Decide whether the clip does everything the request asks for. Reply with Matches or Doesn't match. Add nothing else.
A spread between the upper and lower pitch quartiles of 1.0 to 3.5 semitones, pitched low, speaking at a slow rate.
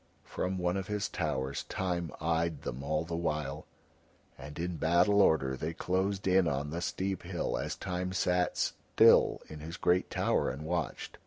Doesn't match